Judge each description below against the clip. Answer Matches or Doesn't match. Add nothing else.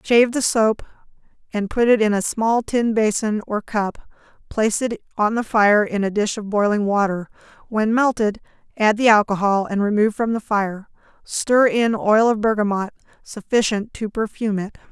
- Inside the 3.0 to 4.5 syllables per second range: Doesn't match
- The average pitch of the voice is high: Matches